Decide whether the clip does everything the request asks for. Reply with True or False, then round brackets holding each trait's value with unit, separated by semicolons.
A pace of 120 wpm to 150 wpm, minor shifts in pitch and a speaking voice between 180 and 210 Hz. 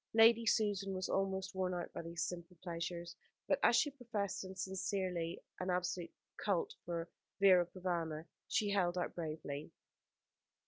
True (145 wpm; 2.3 semitones; 185 Hz)